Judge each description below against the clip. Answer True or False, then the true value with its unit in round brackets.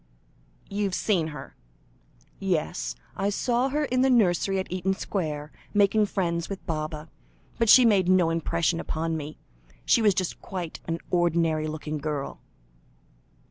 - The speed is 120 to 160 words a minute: True (140 wpm)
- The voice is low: False (175 Hz)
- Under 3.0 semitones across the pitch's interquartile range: False (4.2 semitones)